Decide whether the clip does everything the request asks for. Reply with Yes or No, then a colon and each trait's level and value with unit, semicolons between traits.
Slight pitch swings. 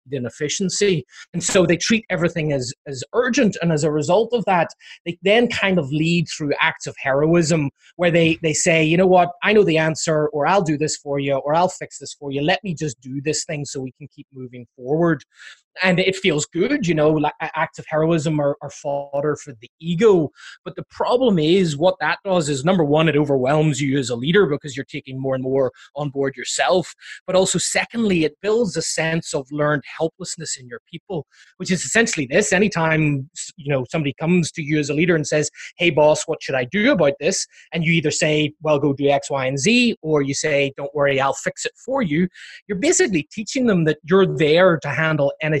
No: average, 3.9 semitones